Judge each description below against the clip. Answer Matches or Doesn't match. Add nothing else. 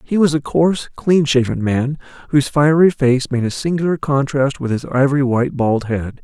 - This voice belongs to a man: Matches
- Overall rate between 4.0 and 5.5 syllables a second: Matches